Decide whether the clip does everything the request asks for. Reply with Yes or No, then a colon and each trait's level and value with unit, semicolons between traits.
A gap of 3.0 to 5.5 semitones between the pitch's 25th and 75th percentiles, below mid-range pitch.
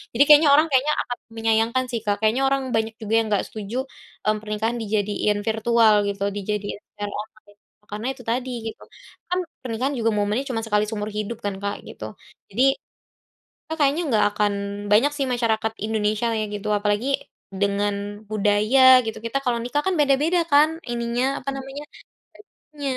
No: average, 3.8 semitones; high, 225 Hz